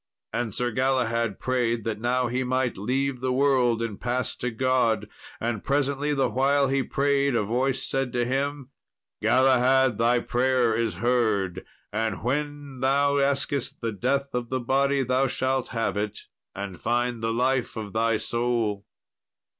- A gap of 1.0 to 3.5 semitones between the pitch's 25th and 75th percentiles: Yes, narrow, 2.5 semitones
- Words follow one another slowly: No, average, 155 wpm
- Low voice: Yes, low, 125 Hz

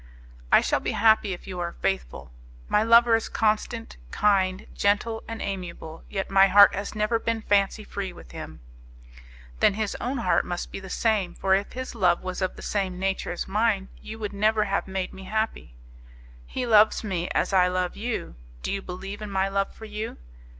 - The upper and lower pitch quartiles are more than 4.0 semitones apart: No, average, 2.7 semitones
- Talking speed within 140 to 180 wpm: No, average, 195 wpm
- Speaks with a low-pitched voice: No, high, 200 Hz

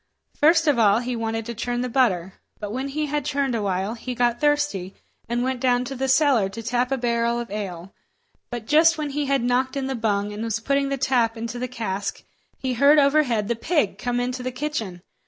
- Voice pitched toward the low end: No, high, 245 Hz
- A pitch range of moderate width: Yes, average, 3.4 semitones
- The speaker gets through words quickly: Yes, fast, 225 wpm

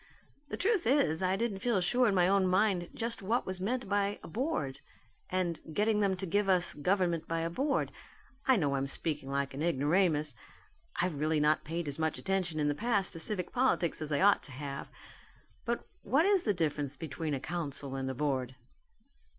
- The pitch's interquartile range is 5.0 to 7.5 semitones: Yes, average, 5.3 semitones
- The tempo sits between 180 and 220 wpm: Yes, average, 200 wpm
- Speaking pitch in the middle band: Yes, medium, 175 Hz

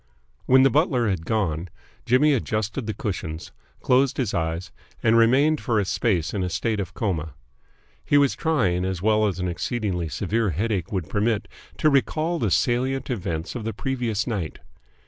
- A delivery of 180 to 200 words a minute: No, average, 170 wpm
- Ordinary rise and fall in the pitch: No, wide, 5.7 semitones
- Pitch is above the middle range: No, low, 110 Hz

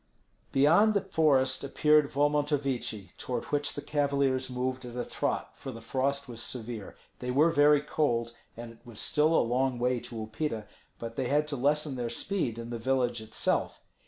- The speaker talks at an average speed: Yes, average, 180 wpm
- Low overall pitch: Yes, low, 130 Hz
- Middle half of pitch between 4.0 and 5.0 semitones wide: No, average, 3.6 semitones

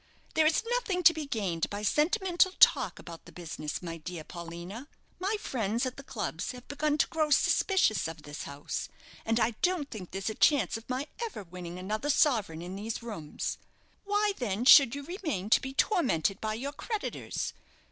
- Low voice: No, high, 235 Hz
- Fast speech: No, average, 180 wpm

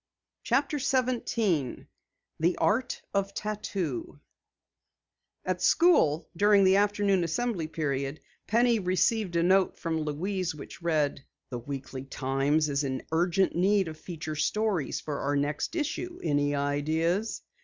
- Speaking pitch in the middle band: Yes, medium, 175 Hz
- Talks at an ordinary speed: No, slow, 125 wpm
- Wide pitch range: Yes, wide, 5.9 semitones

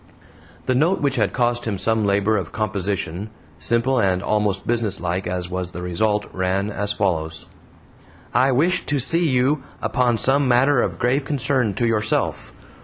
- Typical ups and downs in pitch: Yes, average, 4.9 semitones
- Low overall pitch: Yes, low, 110 Hz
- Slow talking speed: No, average, 160 wpm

